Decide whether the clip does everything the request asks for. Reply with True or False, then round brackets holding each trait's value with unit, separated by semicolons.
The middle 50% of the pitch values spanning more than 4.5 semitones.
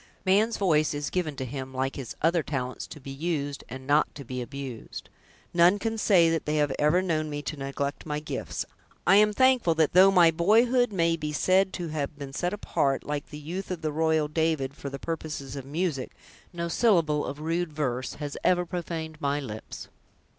False (3.8 semitones)